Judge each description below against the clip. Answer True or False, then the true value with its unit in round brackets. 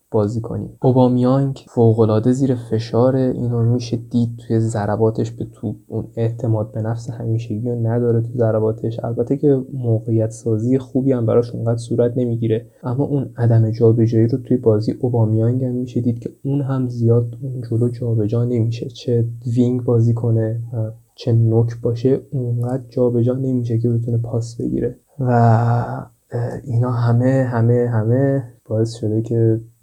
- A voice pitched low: True (120 Hz)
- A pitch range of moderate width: False (1.7 semitones)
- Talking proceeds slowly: False (150 wpm)